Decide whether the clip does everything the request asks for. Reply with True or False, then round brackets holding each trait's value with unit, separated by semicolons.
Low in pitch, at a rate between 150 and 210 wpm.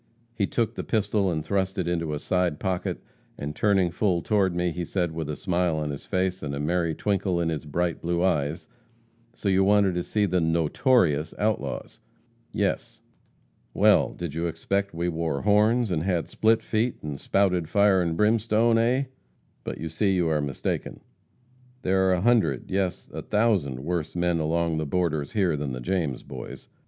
True (90 Hz; 185 wpm)